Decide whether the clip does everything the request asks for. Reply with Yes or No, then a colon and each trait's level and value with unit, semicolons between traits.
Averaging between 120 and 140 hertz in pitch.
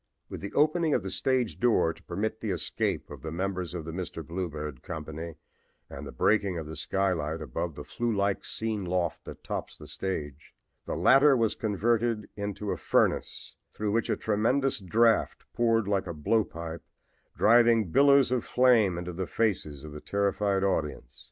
No: low, 100 Hz